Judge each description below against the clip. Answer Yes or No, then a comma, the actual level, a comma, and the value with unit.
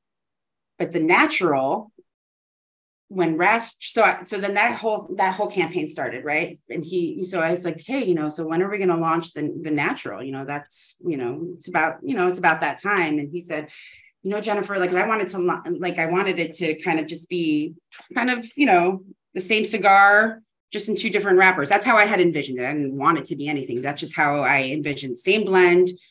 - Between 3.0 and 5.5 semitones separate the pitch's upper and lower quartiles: Yes, average, 4.2 semitones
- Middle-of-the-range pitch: Yes, medium, 180 Hz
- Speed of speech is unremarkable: No, fast, 225 wpm